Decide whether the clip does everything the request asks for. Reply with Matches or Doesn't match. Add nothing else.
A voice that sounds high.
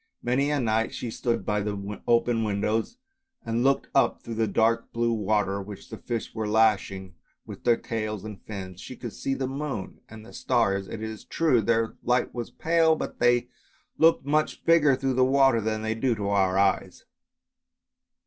Doesn't match